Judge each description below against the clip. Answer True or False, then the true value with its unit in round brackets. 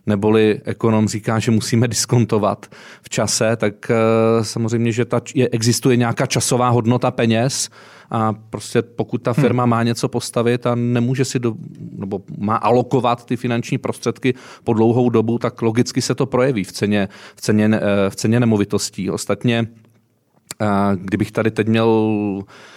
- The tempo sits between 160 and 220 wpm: False (150 wpm)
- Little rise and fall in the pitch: True (2.0 semitones)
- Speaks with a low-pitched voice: True (115 Hz)